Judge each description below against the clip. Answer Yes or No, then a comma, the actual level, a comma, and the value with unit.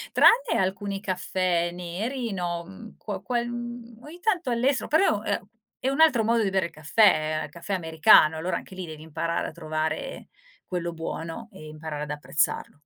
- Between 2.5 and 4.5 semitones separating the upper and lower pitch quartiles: No, wide, 6.3 semitones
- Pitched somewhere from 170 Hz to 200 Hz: Yes, medium, 185 Hz